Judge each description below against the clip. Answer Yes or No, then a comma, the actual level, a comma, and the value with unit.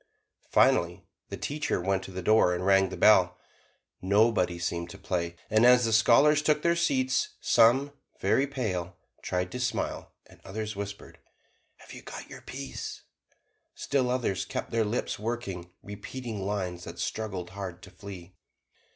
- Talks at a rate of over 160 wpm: No, average, 155 wpm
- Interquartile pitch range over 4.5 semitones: Yes, average, 4.9 semitones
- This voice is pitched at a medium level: No, low, 100 Hz